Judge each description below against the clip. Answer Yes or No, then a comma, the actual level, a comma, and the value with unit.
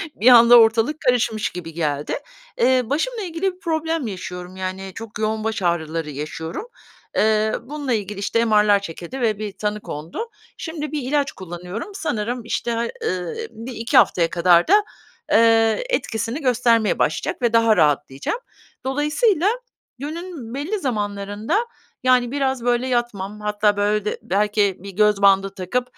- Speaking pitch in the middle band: No, high, 225 Hz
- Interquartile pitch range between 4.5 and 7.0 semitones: Yes, average, 4.8 semitones